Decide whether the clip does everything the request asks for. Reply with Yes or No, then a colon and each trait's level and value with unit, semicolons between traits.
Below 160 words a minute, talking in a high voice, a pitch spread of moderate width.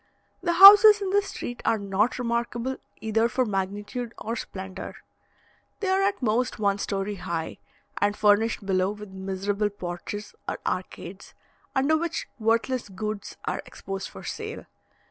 Yes: average, 145 wpm; high, 215 Hz; average, 4.3 semitones